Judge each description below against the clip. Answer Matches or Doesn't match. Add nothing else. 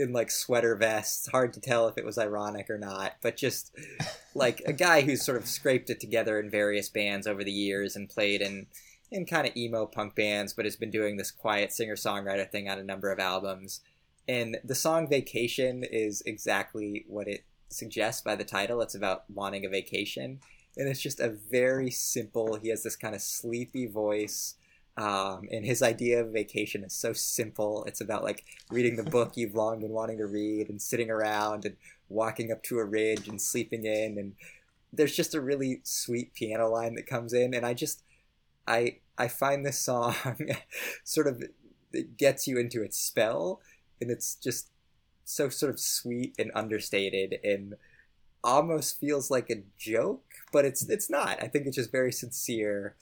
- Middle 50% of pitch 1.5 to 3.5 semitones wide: Matches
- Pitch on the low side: Matches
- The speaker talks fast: Doesn't match